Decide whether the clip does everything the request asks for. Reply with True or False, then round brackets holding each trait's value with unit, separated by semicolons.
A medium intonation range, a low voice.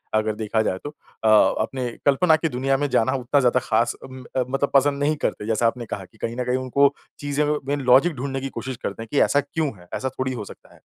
True (3.6 semitones; 130 Hz)